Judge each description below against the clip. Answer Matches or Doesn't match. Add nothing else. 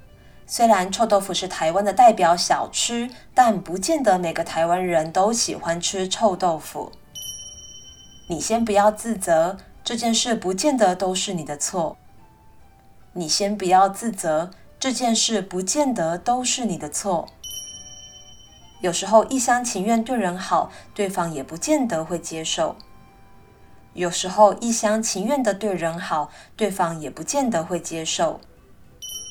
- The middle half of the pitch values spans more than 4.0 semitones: Matches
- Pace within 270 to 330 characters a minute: Doesn't match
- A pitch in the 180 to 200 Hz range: Matches